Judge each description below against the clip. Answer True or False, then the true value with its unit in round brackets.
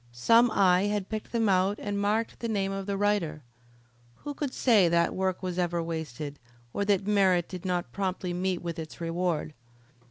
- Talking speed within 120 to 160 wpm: False (185 wpm)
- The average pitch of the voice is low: False (185 Hz)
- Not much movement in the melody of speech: False (3.1 semitones)